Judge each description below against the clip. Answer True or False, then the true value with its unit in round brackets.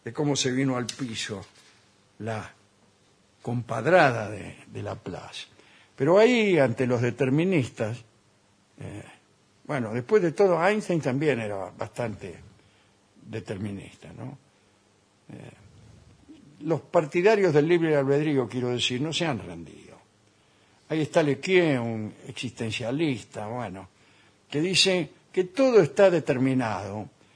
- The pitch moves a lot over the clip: True (6.7 semitones)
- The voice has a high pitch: False (125 Hz)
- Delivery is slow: True (110 wpm)